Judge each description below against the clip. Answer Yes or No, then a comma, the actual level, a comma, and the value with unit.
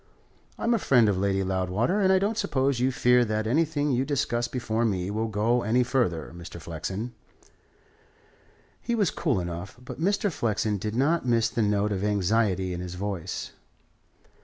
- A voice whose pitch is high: No, low, 115 Hz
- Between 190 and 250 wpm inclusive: No, average, 170 wpm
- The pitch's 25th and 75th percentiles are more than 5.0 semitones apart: Yes, wide, 5.4 semitones